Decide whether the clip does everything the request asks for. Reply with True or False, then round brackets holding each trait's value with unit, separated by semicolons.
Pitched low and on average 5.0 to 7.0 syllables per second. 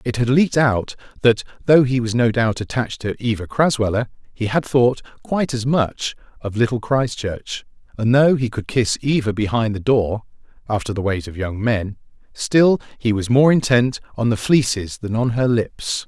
False (120 Hz; 4.8 syllables/s)